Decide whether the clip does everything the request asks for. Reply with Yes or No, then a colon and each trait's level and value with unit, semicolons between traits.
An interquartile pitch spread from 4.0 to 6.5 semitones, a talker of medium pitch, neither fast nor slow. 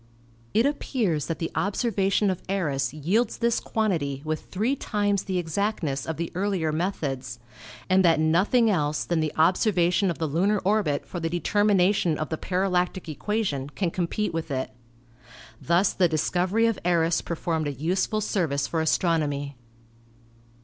Yes: average, 4.3 semitones; medium, 175 Hz; average, 155 wpm